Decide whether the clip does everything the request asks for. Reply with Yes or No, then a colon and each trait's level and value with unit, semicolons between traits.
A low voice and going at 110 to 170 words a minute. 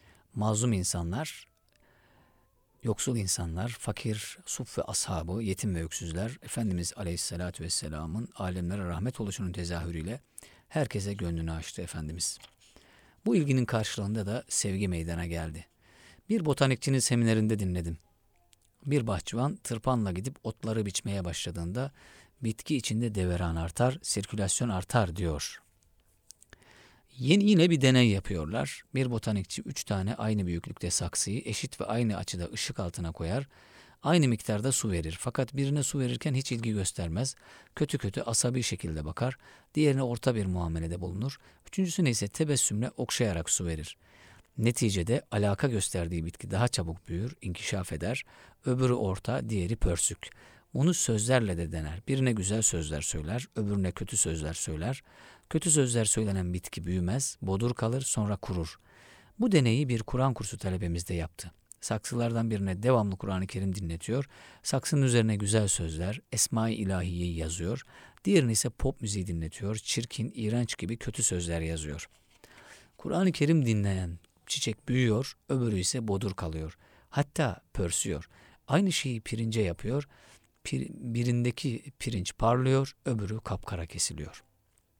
Yes: low, 110 Hz; average, 125 wpm